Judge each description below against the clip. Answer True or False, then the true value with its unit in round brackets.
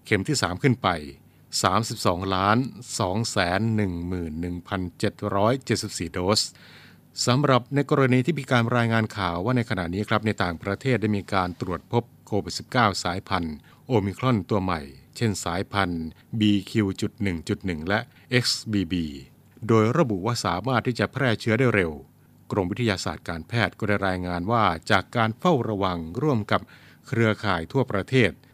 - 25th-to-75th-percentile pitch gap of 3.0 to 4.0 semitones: False (4.4 semitones)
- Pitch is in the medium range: False (105 Hz)